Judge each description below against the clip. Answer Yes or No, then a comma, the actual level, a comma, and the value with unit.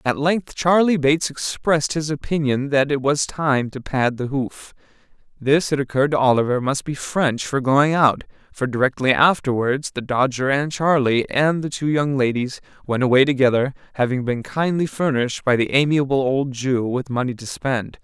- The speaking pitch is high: No, low, 135 Hz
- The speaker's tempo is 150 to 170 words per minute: No, average, 180 wpm